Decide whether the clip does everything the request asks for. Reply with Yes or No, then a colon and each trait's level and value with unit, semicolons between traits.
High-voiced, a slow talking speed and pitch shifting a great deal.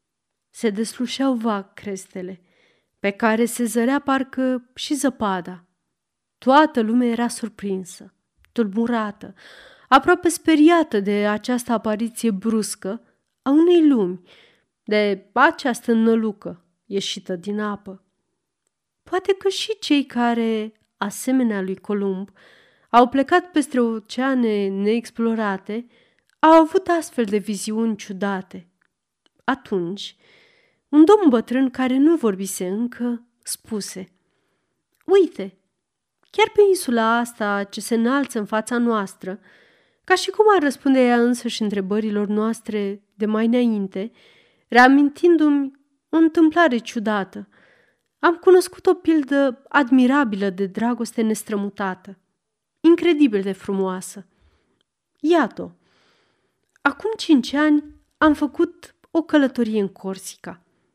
Yes: high, 230 Hz; slow, 105 wpm; wide, 5.9 semitones